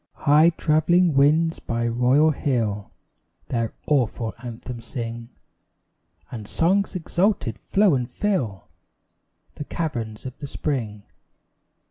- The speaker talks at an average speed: No, slow, 105 wpm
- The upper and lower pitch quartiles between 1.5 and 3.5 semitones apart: No, wide, 5.6 semitones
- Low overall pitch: Yes, low, 130 Hz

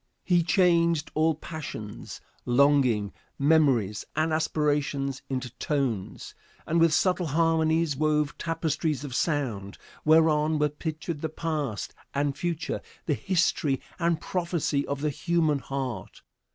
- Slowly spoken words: Yes, slow, 120 wpm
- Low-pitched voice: No, medium, 150 Hz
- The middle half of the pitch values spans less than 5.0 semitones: Yes, average, 2.8 semitones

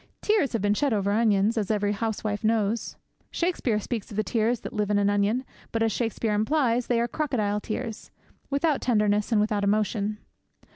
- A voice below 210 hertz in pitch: No, high, 215 Hz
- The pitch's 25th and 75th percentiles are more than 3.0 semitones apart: No, narrow, 2.5 semitones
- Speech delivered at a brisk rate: No, average, 185 wpm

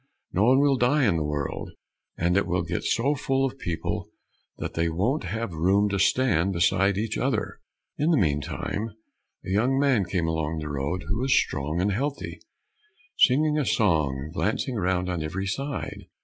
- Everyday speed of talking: Yes, average, 180 wpm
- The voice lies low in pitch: Yes, low, 100 Hz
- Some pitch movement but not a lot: No, wide, 7.6 semitones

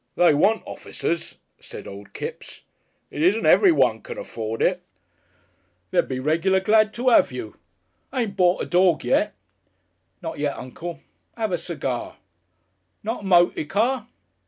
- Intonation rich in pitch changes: Yes, wide, 6.6 semitones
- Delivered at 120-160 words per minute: Yes, average, 140 wpm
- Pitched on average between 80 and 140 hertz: No, medium, 180 Hz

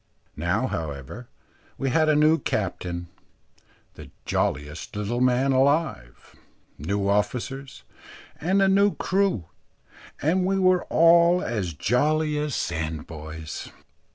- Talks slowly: Yes, slow, 110 wpm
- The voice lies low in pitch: Yes, low, 125 Hz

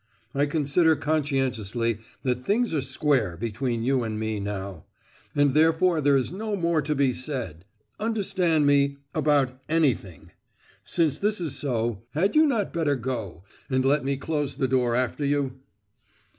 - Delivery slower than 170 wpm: Yes, average, 155 wpm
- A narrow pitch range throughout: No, average, 4.2 semitones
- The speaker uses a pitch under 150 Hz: Yes, medium, 140 Hz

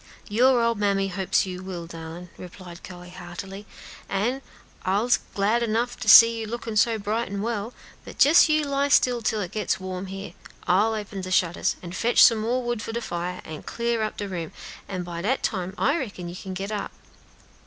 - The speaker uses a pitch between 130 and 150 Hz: No, high, 205 Hz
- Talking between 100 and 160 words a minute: No, average, 200 wpm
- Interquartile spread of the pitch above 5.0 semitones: No, average, 4.1 semitones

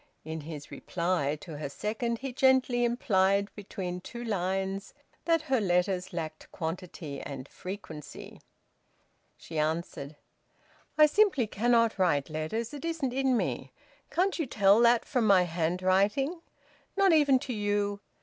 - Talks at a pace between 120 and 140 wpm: Yes, slow, 135 wpm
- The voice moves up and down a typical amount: No, wide, 6.1 semitones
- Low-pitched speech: No, high, 200 Hz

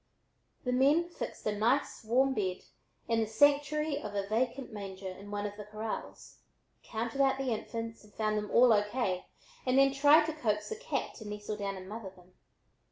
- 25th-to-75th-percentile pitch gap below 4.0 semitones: No, average, 4.6 semitones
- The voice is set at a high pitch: Yes, high, 225 Hz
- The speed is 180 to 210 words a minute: Yes, average, 195 wpm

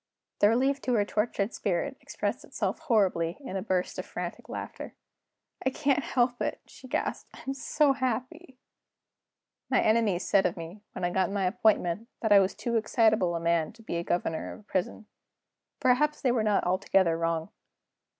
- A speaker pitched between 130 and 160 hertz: No, high, 215 Hz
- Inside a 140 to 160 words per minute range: No, average, 175 wpm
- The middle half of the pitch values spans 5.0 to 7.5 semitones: Yes, wide, 5.6 semitones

